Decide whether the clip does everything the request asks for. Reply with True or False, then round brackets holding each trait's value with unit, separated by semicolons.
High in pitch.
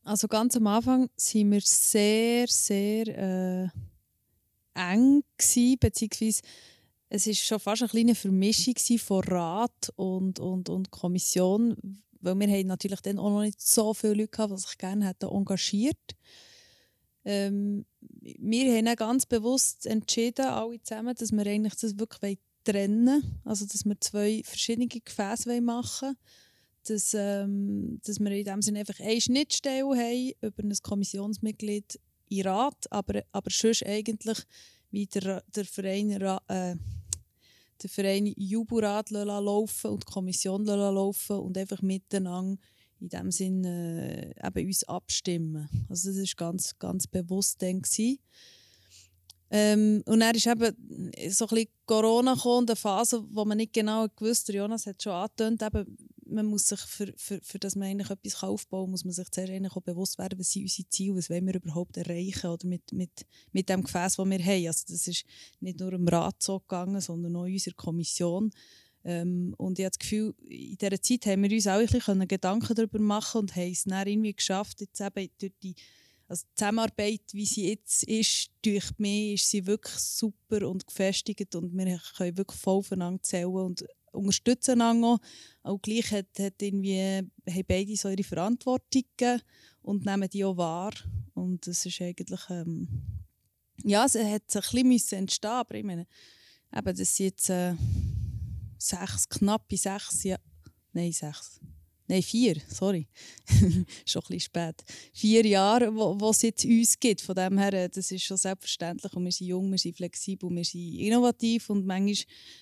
True (200 Hz)